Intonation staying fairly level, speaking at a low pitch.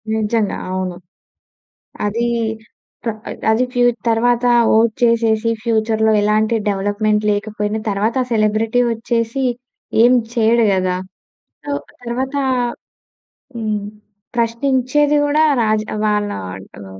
No: narrow, 2.0 semitones; high, 220 Hz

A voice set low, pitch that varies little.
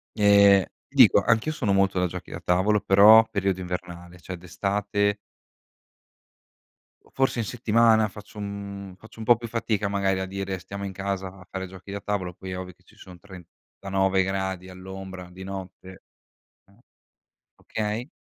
Yes: very low, 95 Hz; narrow, 1.8 semitones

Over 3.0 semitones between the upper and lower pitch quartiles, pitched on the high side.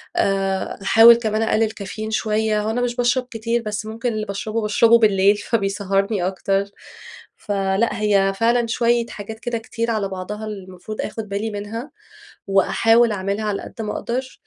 No: narrow, 2.5 semitones; high, 215 Hz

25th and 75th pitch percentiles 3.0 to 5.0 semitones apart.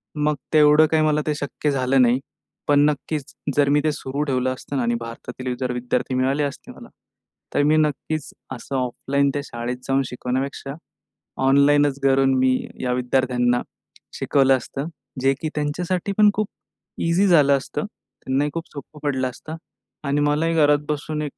No: narrow, 2.5 semitones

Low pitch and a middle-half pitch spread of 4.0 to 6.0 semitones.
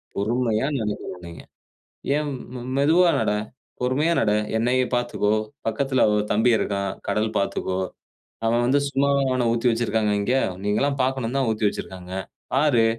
Yes: low, 120 Hz; average, 4.3 semitones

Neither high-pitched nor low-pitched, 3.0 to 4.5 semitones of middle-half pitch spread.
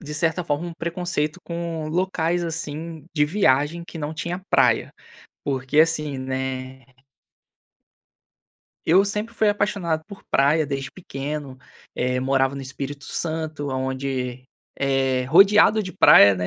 Yes: medium, 150 Hz; average, 4.2 semitones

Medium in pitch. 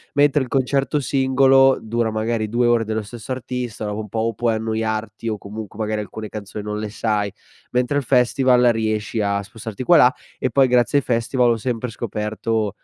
No: low, 115 Hz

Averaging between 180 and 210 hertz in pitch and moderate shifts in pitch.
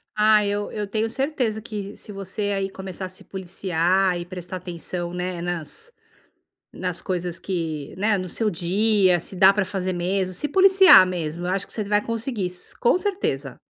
Yes: high, 190 Hz; average, 3.0 semitones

